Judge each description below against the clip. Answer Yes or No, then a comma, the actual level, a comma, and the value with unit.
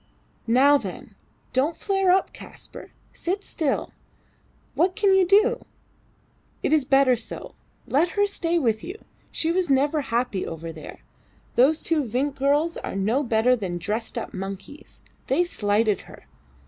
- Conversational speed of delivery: Yes, average, 150 wpm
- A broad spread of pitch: Yes, wide, 7.2 semitones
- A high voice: Yes, very high, 280 Hz